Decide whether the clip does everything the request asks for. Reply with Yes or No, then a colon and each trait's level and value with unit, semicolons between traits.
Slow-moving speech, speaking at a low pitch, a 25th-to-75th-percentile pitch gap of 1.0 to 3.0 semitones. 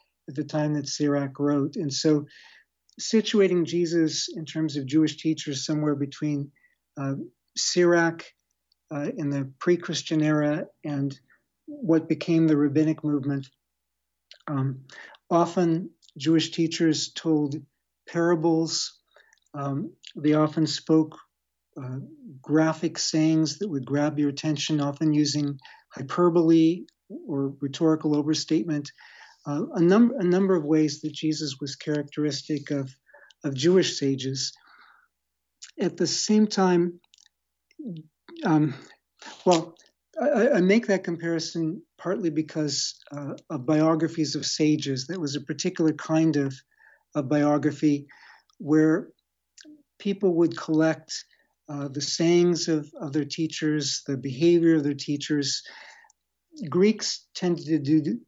No: slow, 120 wpm; medium, 155 Hz; average, 2.7 semitones